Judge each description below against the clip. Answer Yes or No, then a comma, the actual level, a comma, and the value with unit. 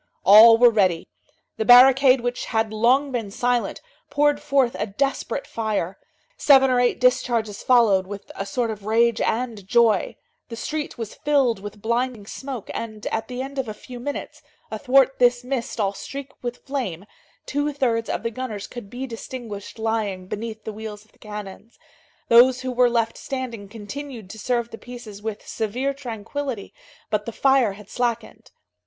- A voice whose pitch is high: Yes, high, 235 Hz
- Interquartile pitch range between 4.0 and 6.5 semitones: No, average, 3.1 semitones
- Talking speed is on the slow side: No, average, 170 wpm